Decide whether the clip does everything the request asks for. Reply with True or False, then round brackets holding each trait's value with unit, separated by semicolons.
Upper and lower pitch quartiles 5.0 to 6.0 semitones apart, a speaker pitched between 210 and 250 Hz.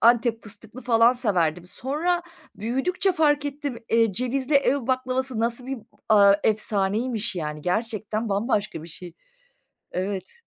False (4.5 semitones; 230 Hz)